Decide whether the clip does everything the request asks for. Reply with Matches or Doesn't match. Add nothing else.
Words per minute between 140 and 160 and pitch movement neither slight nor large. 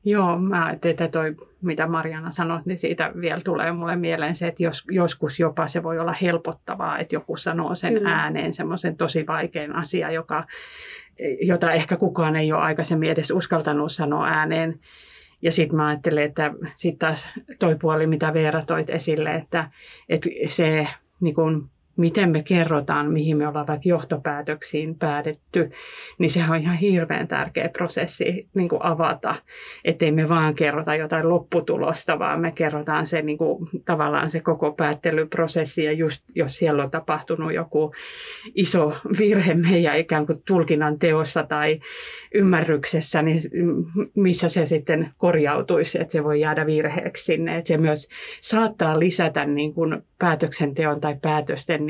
Doesn't match